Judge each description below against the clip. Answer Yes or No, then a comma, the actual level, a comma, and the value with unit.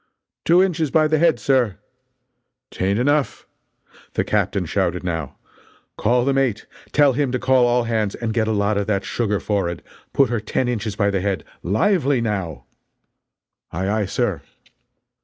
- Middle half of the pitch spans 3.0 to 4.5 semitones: No, average, 5.1 semitones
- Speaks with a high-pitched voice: No, low, 115 Hz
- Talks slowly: No, average, 165 wpm